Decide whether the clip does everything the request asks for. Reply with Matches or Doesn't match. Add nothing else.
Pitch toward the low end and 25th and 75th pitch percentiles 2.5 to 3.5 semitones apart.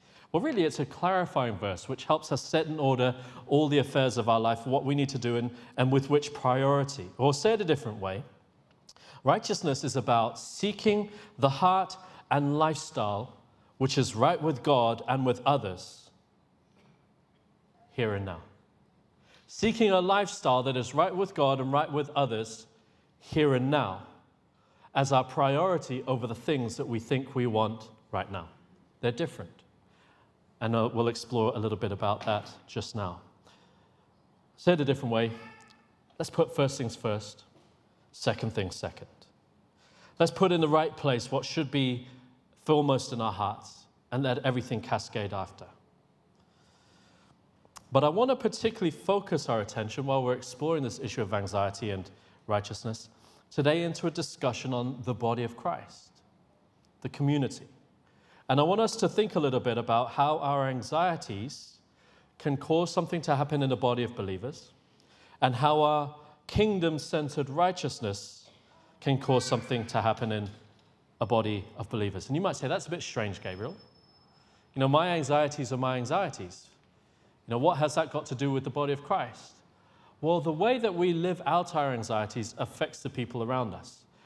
Doesn't match